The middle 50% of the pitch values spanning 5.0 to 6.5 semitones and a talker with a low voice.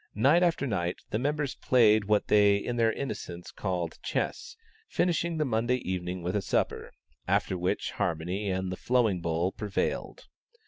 Yes: wide, 5.6 semitones; low, 105 Hz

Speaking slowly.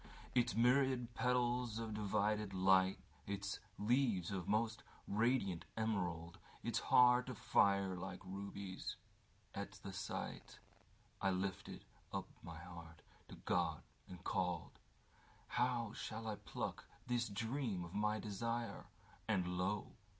Yes: slow, 110 wpm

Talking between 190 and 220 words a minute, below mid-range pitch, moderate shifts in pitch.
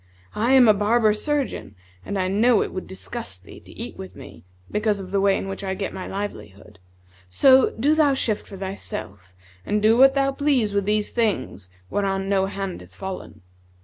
No: average, 195 wpm; high, 200 Hz; average, 3.4 semitones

